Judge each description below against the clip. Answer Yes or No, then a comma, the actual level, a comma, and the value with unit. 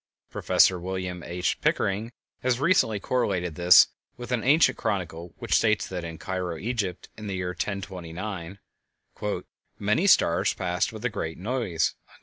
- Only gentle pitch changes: No, average, 3.8 semitones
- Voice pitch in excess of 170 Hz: No, very low, 95 Hz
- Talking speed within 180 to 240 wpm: No, average, 140 wpm